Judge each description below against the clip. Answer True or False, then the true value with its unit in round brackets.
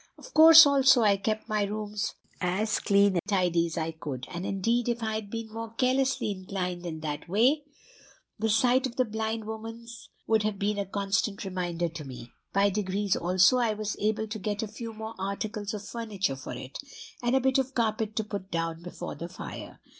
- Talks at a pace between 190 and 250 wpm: True (200 wpm)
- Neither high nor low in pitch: False (210 Hz)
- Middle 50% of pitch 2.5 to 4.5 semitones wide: True (3.4 semitones)